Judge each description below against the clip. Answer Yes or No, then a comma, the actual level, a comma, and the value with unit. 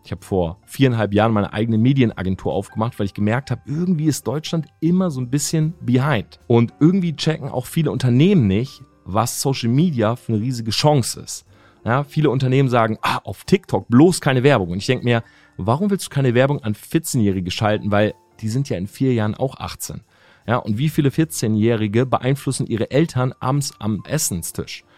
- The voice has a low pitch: Yes, low, 125 Hz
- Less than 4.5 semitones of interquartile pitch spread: No, average, 5.2 semitones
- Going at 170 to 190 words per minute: Yes, average, 185 wpm